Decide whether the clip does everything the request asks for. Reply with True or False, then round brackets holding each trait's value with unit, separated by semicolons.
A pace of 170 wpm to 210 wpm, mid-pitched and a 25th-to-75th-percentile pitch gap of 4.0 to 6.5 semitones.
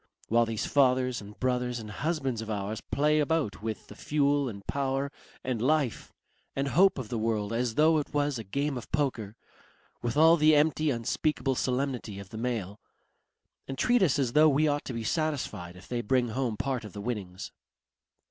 False (190 wpm; 130 Hz; 4.6 semitones)